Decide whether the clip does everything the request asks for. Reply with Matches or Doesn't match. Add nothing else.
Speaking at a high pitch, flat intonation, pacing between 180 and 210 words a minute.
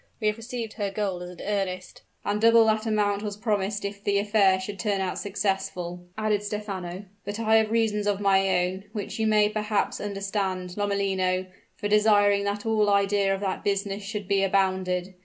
Matches